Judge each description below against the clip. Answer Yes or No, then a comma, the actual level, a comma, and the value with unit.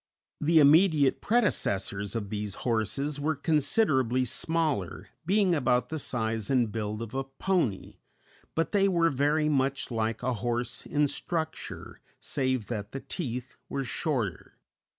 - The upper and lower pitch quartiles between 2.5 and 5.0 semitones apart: No, wide, 5.5 semitones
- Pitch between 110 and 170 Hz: Yes, low, 135 Hz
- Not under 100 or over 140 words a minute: Yes, slow, 135 wpm